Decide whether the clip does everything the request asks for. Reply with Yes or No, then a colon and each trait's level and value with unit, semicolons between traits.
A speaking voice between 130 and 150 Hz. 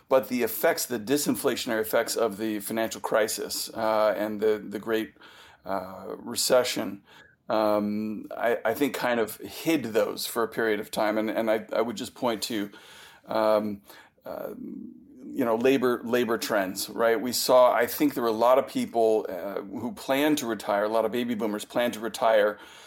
No: low, 115 Hz